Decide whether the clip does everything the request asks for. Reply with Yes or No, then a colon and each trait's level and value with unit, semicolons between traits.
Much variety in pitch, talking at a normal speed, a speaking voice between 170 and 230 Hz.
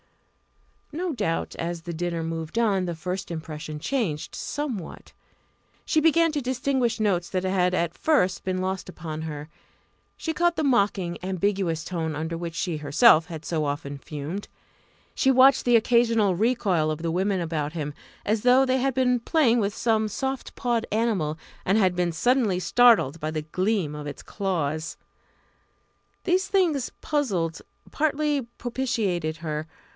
Yes: wide, 7.0 semitones; average, 155 wpm; high, 190 Hz